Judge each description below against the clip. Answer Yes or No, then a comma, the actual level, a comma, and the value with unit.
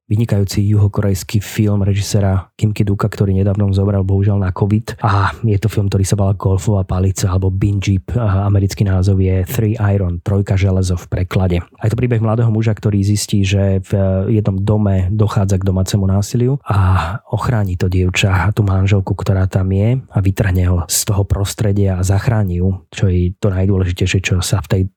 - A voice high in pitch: No, low, 100 Hz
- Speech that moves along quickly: Yes, fast, 180 wpm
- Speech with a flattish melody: Yes, narrow, 1.9 semitones